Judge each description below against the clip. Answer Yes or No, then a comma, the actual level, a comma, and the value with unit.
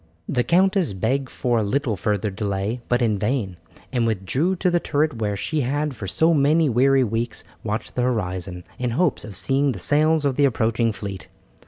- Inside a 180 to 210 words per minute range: Yes, average, 190 wpm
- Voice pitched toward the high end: No, low, 120 Hz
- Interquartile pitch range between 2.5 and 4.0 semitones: No, wide, 5.4 semitones